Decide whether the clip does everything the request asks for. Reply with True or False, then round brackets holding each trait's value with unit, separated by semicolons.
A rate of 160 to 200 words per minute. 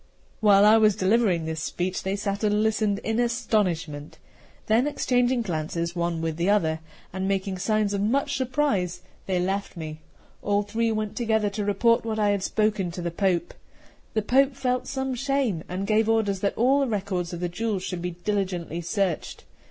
True (185 wpm)